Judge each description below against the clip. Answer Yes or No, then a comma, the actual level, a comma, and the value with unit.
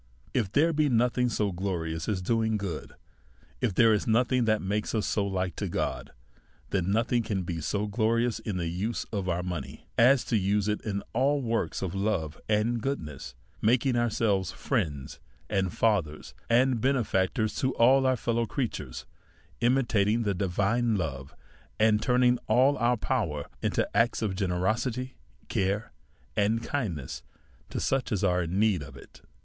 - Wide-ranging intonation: No, average, 4.2 semitones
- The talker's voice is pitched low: Yes, low, 110 Hz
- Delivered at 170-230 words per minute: No, average, 160 wpm